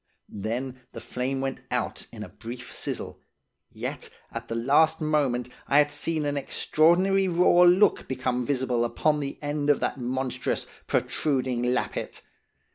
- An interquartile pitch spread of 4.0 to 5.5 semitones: No, average, 3.4 semitones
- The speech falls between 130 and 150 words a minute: Yes, average, 145 wpm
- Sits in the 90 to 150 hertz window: Yes, low, 135 Hz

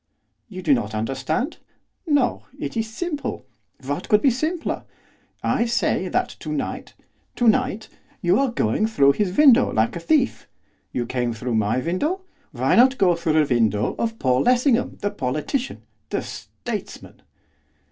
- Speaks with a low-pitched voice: No, high, 205 Hz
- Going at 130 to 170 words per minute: Yes, average, 150 wpm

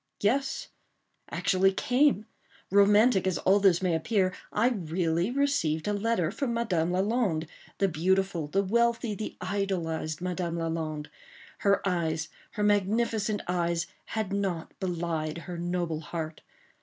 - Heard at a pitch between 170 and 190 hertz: Yes, medium, 185 Hz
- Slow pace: Yes, slow, 120 wpm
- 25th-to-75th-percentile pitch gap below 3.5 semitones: No, average, 3.8 semitones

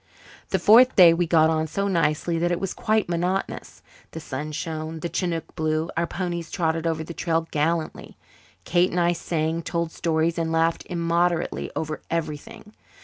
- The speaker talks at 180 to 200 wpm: No, average, 170 wpm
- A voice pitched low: No, medium, 165 Hz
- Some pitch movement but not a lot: No, narrow, 1.5 semitones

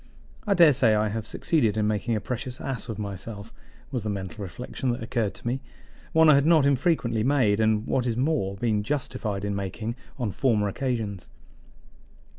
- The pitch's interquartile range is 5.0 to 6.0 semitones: No, average, 4.0 semitones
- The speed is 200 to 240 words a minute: No, average, 180 wpm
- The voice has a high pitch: No, low, 115 Hz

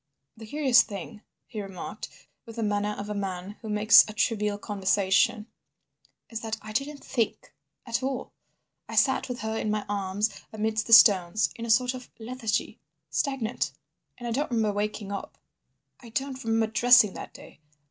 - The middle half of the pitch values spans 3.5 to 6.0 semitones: No, average, 2.7 semitones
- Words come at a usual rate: Yes, average, 160 wpm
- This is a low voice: No, high, 220 Hz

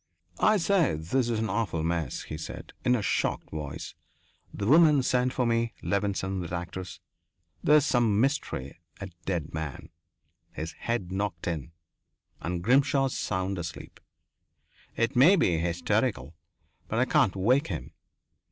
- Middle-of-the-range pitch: No, low, 100 Hz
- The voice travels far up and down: Yes, wide, 6.9 semitones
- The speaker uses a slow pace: No, average, 145 wpm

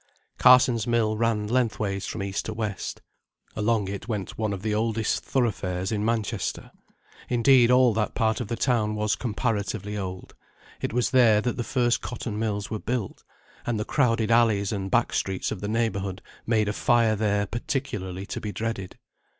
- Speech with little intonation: Yes, narrow, 2.3 semitones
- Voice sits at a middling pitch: No, low, 110 Hz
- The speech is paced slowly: No, average, 175 wpm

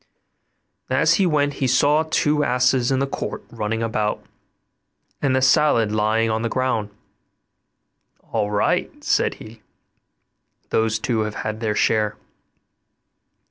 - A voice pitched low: Yes, low, 115 Hz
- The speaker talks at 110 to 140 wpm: Yes, slow, 135 wpm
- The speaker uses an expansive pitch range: No, average, 3.7 semitones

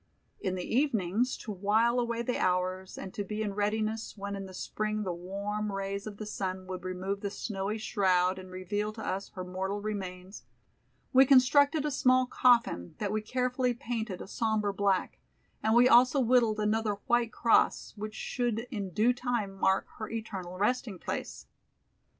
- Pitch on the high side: Yes, high, 210 Hz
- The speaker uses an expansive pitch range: No, average, 3.5 semitones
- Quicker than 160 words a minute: Yes, average, 175 wpm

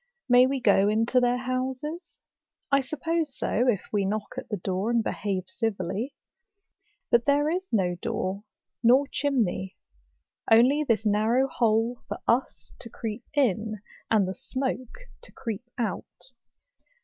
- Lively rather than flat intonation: No, average, 3.9 semitones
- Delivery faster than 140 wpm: No, slow, 135 wpm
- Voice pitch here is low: No, high, 235 Hz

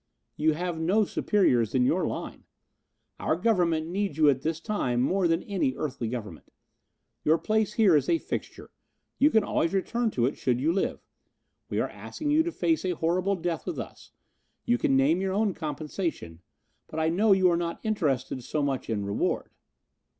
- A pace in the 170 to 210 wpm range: Yes, average, 185 wpm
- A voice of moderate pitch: Yes, medium, 165 Hz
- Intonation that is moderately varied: No, wide, 6.1 semitones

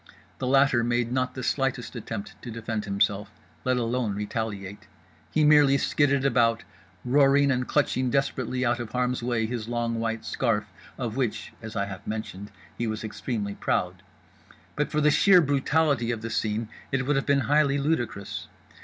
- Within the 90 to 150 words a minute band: No, average, 170 wpm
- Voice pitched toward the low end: Yes, low, 120 Hz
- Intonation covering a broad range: No, average, 3.6 semitones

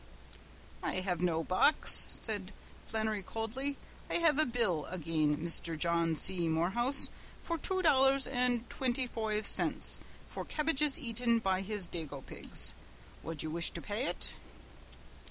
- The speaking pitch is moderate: No, high, 215 Hz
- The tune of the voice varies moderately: No, wide, 7.5 semitones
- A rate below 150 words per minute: Yes, average, 140 wpm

